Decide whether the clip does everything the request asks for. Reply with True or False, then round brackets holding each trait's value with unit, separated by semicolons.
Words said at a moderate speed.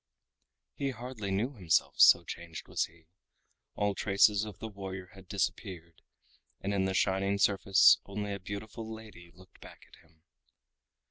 True (150 wpm)